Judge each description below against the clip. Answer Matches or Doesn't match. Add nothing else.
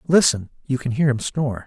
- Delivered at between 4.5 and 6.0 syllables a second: Matches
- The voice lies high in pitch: Doesn't match